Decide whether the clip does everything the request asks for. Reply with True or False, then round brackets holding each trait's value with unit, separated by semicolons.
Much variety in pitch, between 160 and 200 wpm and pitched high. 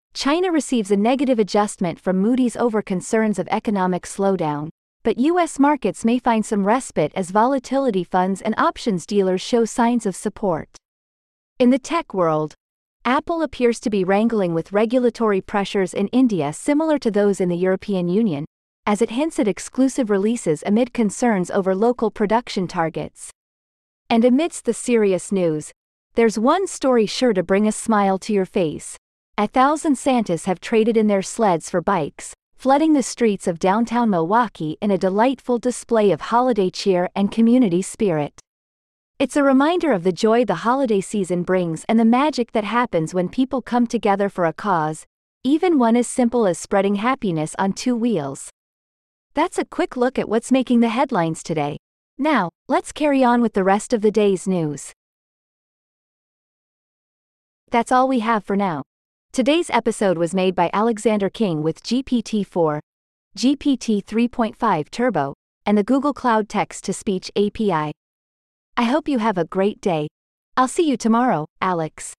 False (4.8 semitones; 165 wpm; 220 Hz)